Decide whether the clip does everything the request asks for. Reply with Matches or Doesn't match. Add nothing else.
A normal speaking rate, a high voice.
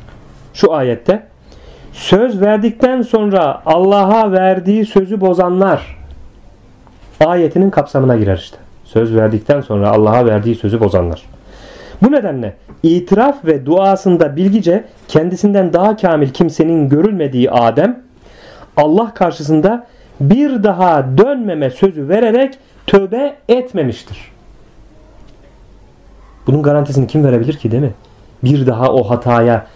Doesn't match